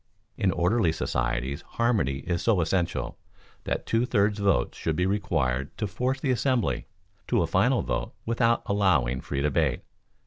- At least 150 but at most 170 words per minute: Yes, average, 160 wpm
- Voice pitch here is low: Yes, very low, 95 Hz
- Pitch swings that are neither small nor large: No, wide, 8.1 semitones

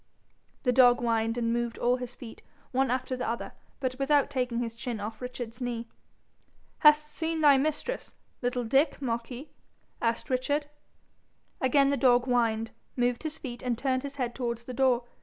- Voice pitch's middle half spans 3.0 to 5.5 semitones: No, narrow, 2.4 semitones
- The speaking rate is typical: Yes, average, 170 wpm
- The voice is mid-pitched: No, very high, 250 Hz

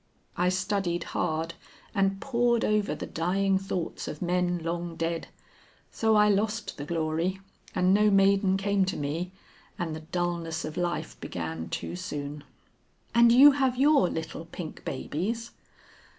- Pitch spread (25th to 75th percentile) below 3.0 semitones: No, average, 3.8 semitones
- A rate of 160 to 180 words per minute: No, average, 145 wpm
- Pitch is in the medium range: Yes, medium, 180 Hz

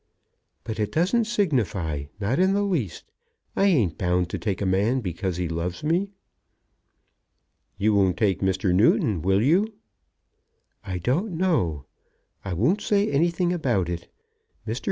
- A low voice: Yes, low, 110 Hz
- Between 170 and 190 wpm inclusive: No, average, 140 wpm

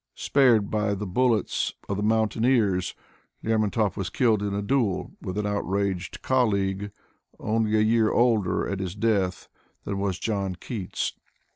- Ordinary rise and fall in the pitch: No, narrow, 2.3 semitones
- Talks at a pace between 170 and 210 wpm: No, average, 145 wpm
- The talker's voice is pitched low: Yes, low, 105 Hz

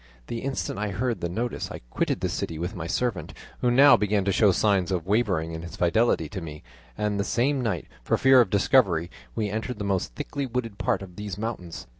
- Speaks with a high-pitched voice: No, low, 105 Hz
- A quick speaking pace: Yes, fast, 220 wpm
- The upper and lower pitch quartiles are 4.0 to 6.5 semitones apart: Yes, average, 4.9 semitones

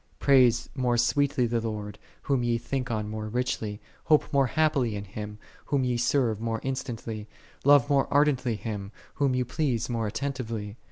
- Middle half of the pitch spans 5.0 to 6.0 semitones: No, average, 3.7 semitones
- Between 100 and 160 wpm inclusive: No, average, 170 wpm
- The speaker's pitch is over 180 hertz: No, low, 120 Hz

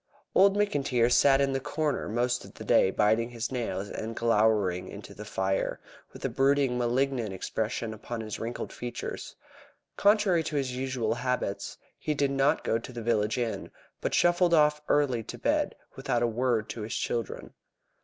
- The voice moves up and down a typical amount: Yes, average, 3.7 semitones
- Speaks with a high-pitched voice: No, low, 120 Hz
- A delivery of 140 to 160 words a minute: No, average, 175 wpm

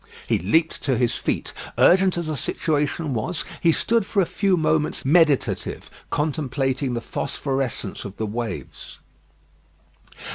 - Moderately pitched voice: Yes, medium, 150 Hz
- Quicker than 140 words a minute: No, slow, 135 wpm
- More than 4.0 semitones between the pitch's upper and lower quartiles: Yes, average, 4.4 semitones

